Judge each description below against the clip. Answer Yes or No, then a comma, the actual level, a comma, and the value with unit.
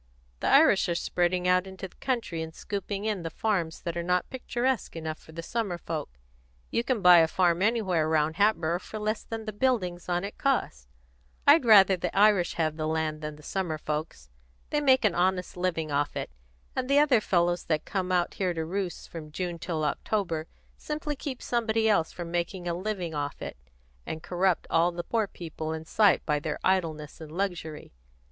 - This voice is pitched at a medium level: Yes, medium, 180 Hz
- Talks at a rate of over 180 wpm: Yes, average, 200 wpm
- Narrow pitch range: No, average, 4.5 semitones